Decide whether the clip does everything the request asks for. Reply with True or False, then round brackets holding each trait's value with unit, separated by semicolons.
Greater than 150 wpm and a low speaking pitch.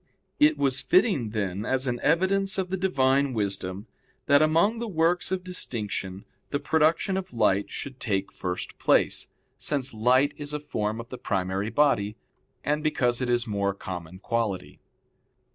True (160 wpm; 130 Hz)